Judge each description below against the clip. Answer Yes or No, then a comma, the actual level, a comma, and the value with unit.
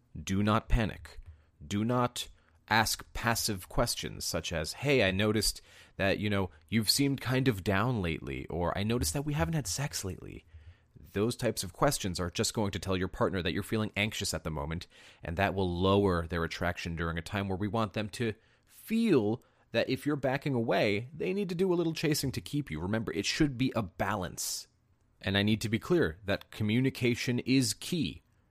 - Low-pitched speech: Yes, low, 105 Hz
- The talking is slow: No, average, 200 wpm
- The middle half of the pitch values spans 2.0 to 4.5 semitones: No, average, 5.2 semitones